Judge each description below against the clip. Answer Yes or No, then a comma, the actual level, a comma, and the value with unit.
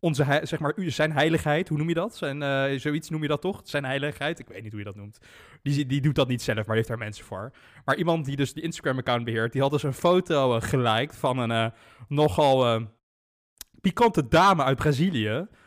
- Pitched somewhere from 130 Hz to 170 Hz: Yes, medium, 140 Hz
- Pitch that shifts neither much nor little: Yes, average, 4.8 semitones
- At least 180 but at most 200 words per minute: No, fast, 225 wpm